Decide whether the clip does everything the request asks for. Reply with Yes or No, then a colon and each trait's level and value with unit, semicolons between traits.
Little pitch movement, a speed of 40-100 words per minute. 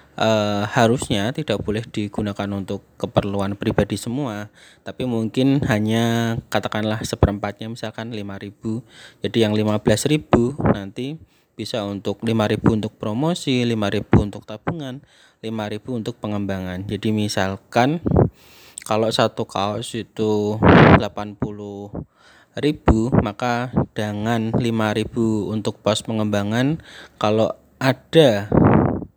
Yes: narrow, 2.3 semitones; average, 95 wpm